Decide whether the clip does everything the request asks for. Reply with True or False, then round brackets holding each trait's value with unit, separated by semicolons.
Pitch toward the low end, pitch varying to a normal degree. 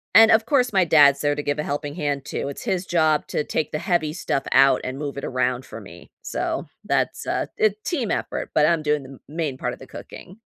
False (150 Hz; 3.8 semitones)